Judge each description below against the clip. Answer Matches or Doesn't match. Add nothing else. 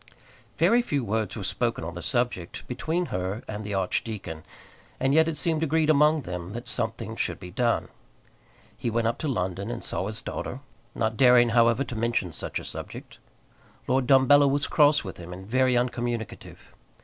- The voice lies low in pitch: Matches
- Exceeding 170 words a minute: Matches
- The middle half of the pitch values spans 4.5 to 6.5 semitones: Matches